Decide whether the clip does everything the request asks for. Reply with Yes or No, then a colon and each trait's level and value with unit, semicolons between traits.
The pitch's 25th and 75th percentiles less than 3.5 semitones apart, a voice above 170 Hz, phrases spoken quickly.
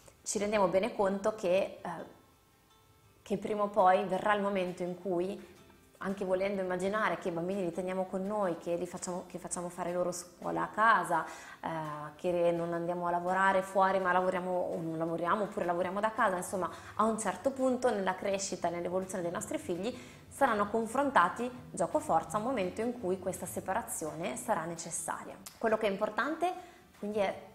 Yes: average, 3.0 semitones; medium, 185 Hz; fast, 175 wpm